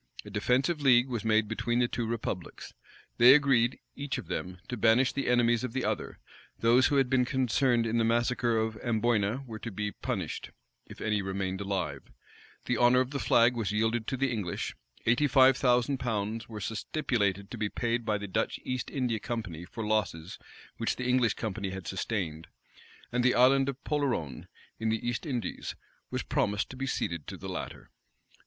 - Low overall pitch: Yes, low, 115 Hz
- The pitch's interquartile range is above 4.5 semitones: No, average, 3.3 semitones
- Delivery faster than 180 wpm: Yes, average, 190 wpm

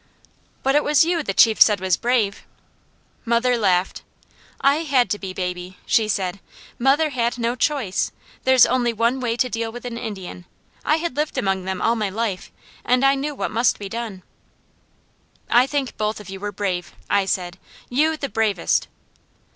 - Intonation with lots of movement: No, average, 4.9 semitones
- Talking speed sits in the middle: Yes, average, 180 wpm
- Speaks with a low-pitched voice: No, high, 230 Hz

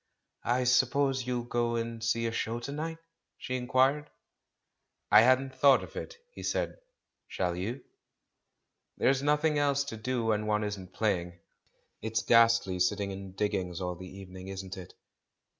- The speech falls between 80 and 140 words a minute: No, average, 155 wpm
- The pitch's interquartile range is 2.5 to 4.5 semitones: No, average, 5.1 semitones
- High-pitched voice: No, low, 115 Hz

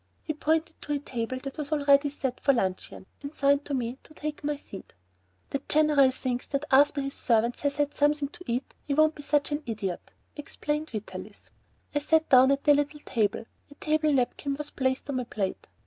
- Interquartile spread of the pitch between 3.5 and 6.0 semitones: No, narrow, 2.5 semitones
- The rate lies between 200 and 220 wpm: Yes, fast, 205 wpm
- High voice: Yes, very high, 280 Hz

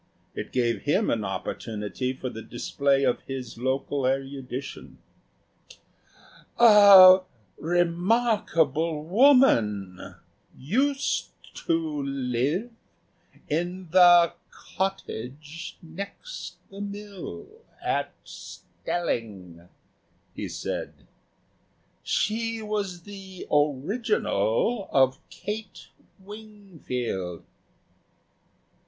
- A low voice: No, medium, 165 Hz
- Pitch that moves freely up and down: Yes, wide, 7.8 semitones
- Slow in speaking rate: Yes, slow, 75 wpm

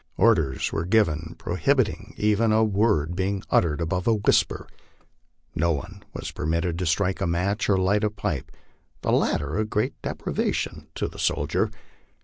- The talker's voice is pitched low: Yes, very low, 95 Hz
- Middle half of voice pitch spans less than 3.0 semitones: No, average, 4.1 semitones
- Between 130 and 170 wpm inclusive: Yes, average, 155 wpm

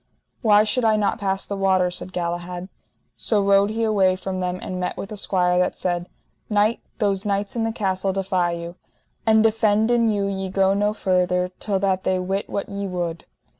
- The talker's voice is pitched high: Yes, high, 195 Hz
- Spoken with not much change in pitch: Yes, narrow, 2.3 semitones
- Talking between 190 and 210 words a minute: Yes, average, 195 wpm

